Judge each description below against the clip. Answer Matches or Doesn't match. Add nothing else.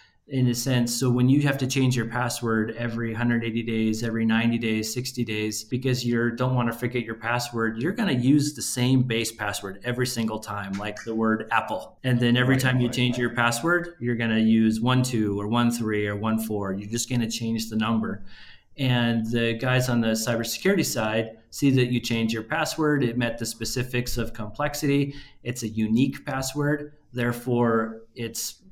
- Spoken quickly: Doesn't match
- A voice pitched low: Matches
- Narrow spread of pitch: Matches